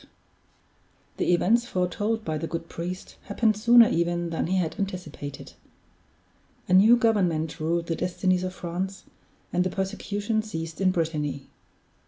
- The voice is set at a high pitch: No, medium, 180 Hz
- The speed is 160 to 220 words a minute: No, average, 140 wpm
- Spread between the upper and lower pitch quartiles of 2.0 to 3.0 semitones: No, average, 3.5 semitones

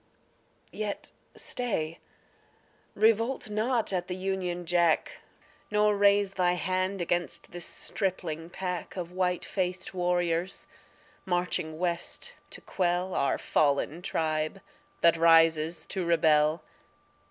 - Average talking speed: No, slow, 105 wpm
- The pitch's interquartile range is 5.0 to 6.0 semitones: No, narrow, 2.4 semitones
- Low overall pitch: No, medium, 180 Hz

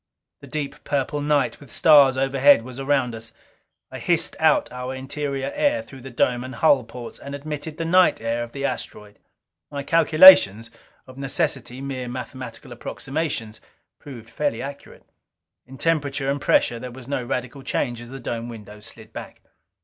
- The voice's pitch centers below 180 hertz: Yes, low, 135 Hz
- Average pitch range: Yes, average, 3.0 semitones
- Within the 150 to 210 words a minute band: Yes, average, 165 wpm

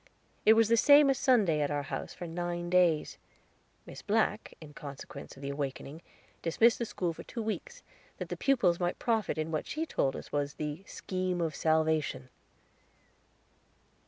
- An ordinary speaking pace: Yes, average, 170 wpm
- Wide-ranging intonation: Yes, wide, 6.6 semitones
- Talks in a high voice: No, medium, 175 Hz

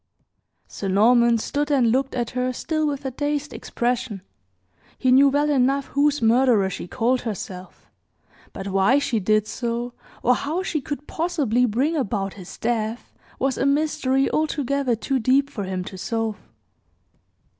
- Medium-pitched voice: No, very high, 250 Hz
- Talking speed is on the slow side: No, average, 155 wpm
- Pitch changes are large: No, average, 4.1 semitones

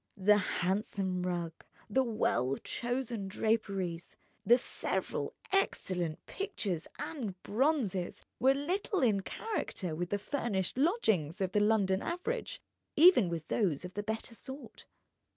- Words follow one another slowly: Yes, slow, 125 wpm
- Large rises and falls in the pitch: Yes, wide, 6.4 semitones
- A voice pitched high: Yes, high, 210 Hz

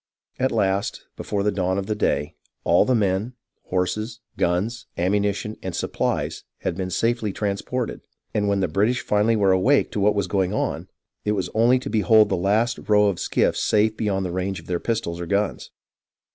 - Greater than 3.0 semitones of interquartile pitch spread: No, average, 2.7 semitones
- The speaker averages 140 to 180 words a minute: No, average, 190 wpm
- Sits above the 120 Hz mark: No, low, 100 Hz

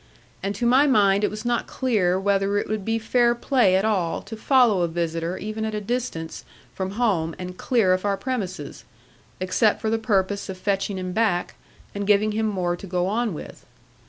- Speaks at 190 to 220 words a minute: Yes, average, 200 wpm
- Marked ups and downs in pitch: No, average, 3.2 semitones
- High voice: Yes, high, 200 Hz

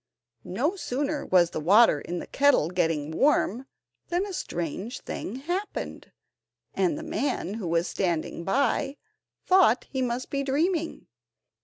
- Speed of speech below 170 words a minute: Yes, average, 140 wpm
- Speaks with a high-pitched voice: Yes, very high, 255 Hz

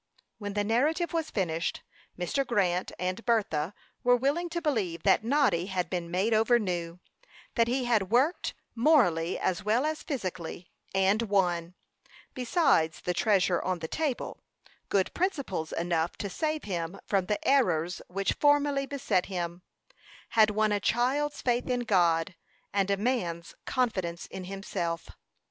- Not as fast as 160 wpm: Yes, average, 150 wpm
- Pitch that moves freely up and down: Yes, wide, 6.0 semitones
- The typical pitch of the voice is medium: No, high, 200 Hz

